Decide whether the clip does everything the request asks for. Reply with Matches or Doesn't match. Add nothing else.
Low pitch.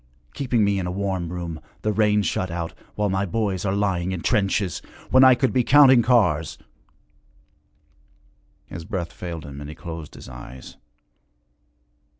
Matches